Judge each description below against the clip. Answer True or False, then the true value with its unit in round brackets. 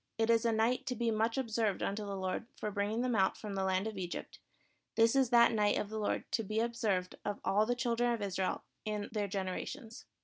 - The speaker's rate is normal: False (235 wpm)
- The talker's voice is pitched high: True (215 Hz)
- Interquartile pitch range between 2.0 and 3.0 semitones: True (2.5 semitones)